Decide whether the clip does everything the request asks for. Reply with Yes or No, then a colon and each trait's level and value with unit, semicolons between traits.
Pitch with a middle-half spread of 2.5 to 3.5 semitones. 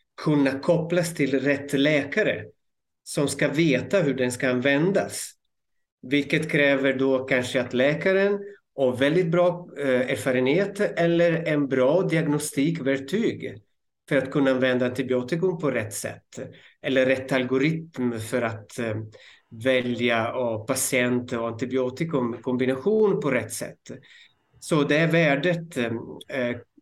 No: average, 4.3 semitones